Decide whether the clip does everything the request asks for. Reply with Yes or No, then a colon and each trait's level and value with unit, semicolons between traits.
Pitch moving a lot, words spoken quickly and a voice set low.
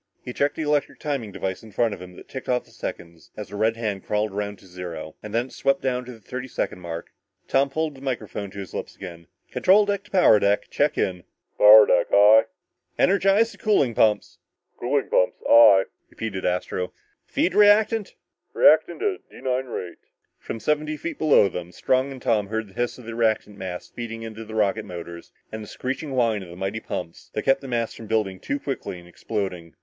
Yes: wide, 5.7 semitones; fast, 210 wpm; low, 110 Hz